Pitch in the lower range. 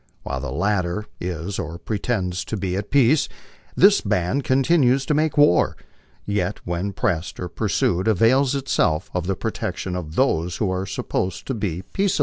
Yes: low, 100 Hz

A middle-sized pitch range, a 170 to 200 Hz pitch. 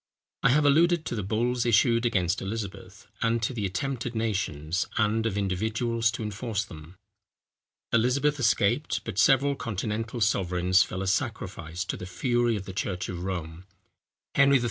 No: average, 4.4 semitones; low, 110 Hz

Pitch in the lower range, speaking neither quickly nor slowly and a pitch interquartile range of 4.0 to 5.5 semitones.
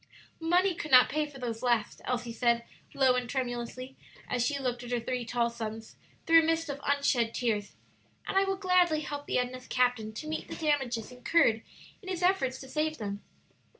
No: very high, 255 Hz; average, 195 wpm; average, 4.5 semitones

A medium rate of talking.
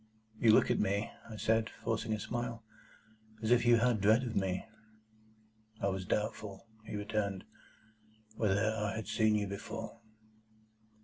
Yes: average, 150 wpm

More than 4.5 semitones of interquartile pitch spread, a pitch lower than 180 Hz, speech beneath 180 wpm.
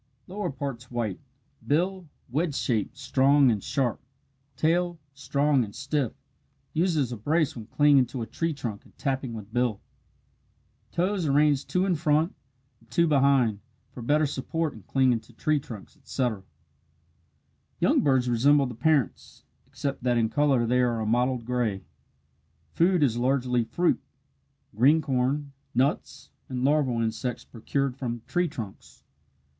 No: average, 3.8 semitones; low, 135 Hz; average, 145 wpm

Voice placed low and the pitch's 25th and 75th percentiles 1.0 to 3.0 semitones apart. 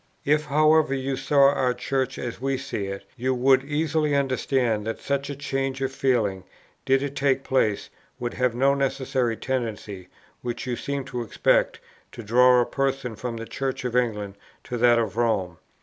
Yes: low, 130 Hz; narrow, 2.6 semitones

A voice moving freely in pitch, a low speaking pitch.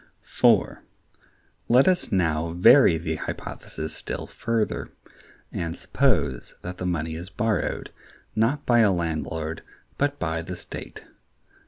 Yes: wide, 5.8 semitones; very low, 90 Hz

